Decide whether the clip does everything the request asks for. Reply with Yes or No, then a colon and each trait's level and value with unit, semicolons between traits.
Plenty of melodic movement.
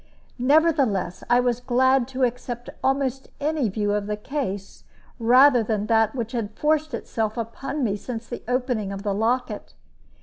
No: average, 3.7 semitones